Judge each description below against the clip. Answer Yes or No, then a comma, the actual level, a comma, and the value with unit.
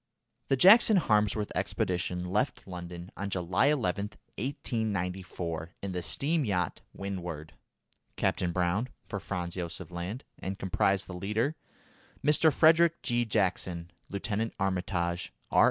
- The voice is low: Yes, very low, 95 Hz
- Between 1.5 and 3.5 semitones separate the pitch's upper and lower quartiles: No, average, 4.3 semitones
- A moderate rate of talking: No, slow, 120 wpm